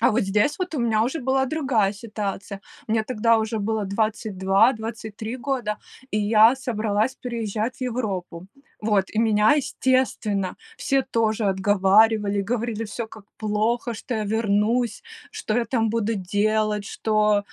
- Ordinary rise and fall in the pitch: No, narrow, 2.3 semitones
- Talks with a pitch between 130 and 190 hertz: No, high, 220 Hz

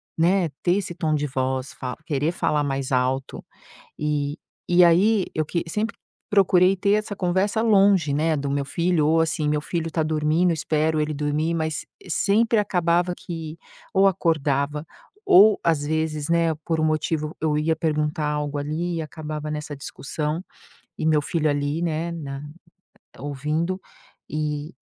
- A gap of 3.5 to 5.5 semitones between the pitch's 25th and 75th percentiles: No, average, 2.7 semitones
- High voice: No, medium, 155 Hz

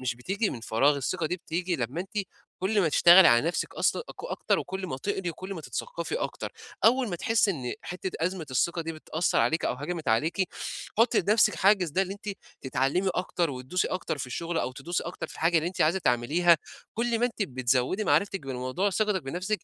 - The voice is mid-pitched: Yes, medium, 175 Hz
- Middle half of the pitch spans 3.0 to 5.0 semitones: No, wide, 5.5 semitones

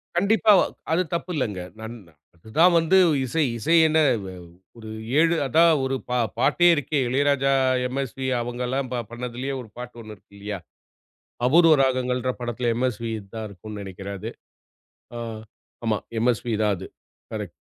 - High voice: No, low, 125 Hz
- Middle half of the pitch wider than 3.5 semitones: Yes, average, 4.6 semitones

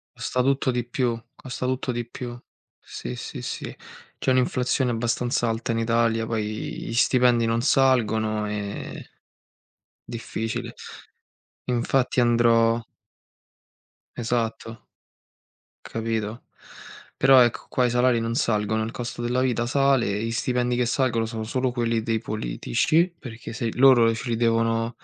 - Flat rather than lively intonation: Yes, narrow, 1.7 semitones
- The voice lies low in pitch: Yes, low, 120 Hz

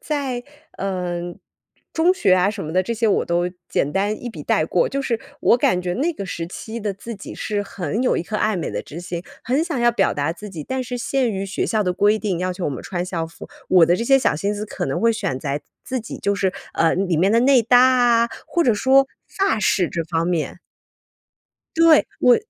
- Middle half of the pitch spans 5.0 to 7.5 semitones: Yes, wide, 5.5 semitones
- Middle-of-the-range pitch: No, high, 205 Hz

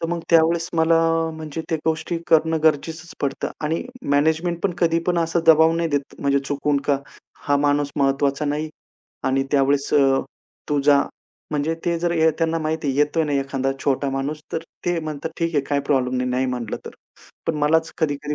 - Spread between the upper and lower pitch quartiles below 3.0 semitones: Yes, narrow, 2.6 semitones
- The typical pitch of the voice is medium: Yes, medium, 150 Hz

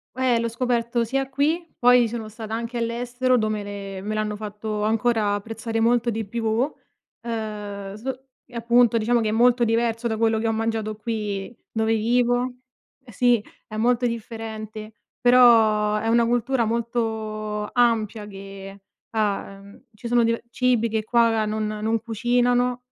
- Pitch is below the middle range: No, high, 225 Hz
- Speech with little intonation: Yes, narrow, 2.0 semitones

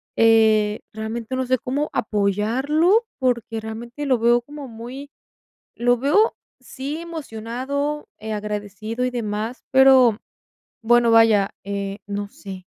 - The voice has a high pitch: Yes, high, 235 Hz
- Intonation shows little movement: No, average, 3.6 semitones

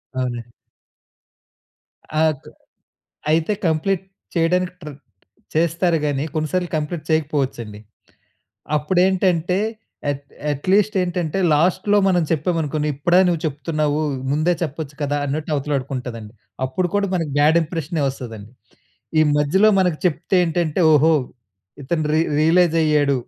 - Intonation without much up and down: No, average, 3.5 semitones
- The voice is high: No, medium, 155 Hz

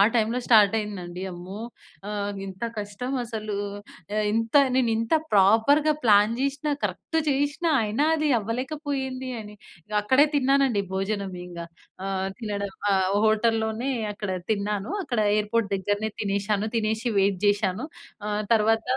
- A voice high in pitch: Yes, high, 215 Hz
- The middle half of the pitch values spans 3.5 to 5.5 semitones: Yes, average, 3.8 semitones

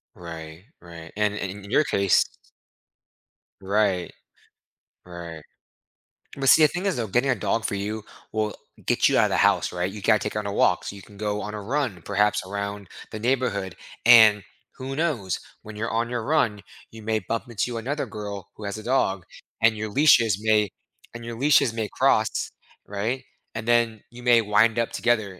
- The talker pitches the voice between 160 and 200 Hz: No, low, 105 Hz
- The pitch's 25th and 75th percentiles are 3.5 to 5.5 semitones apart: No, average, 2.8 semitones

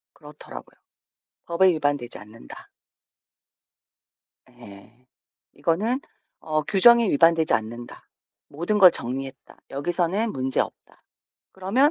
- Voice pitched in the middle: Yes, medium, 155 Hz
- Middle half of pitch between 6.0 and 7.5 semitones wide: Yes, wide, 6.5 semitones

